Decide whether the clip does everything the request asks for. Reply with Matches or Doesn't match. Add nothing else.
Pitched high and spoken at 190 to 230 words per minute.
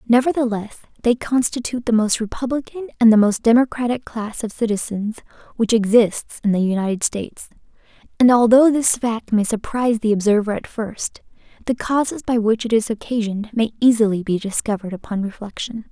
Doesn't match